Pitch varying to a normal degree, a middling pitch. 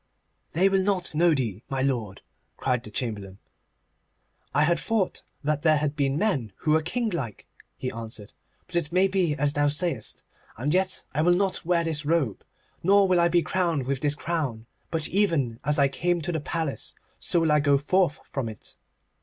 Yes: average, 4.5 semitones; medium, 150 Hz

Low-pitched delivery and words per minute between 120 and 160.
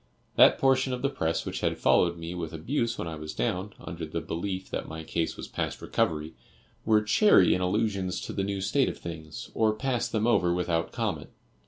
No: very low, 95 Hz; fast, 205 wpm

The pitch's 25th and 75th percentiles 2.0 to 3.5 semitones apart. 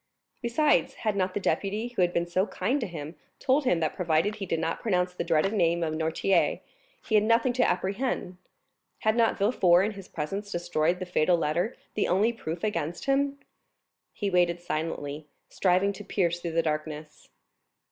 No: average, 4.2 semitones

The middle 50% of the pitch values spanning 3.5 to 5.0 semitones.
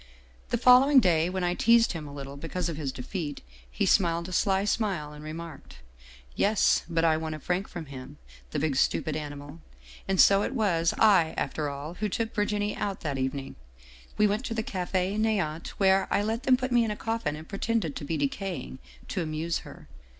No: wide, 5.6 semitones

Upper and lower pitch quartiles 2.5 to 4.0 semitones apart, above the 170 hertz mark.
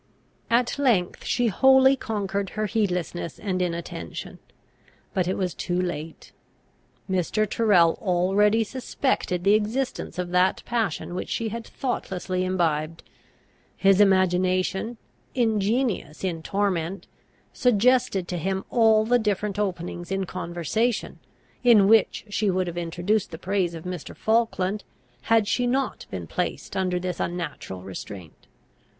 Yes: average, 3.7 semitones; high, 190 Hz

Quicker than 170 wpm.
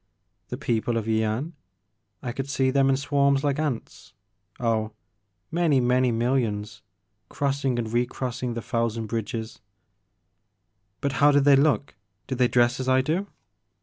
No: average, 155 wpm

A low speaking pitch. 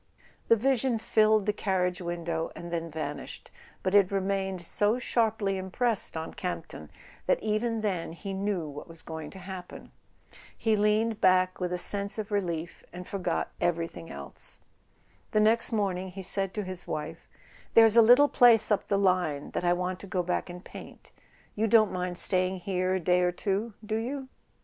No: high, 190 Hz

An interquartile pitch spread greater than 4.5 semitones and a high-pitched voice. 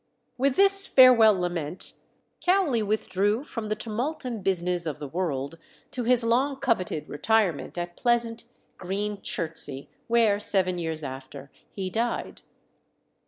Yes: wide, 5.5 semitones; high, 205 Hz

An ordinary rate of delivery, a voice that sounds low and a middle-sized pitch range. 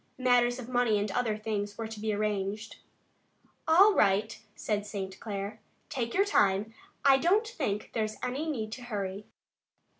No: average, 155 wpm; high, 220 Hz; average, 3.3 semitones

